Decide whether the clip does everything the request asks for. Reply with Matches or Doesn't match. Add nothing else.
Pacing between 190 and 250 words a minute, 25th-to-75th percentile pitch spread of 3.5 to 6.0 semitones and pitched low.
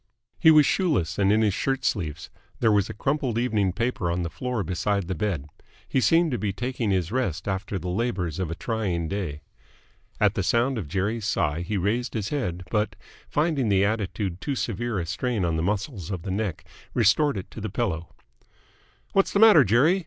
Matches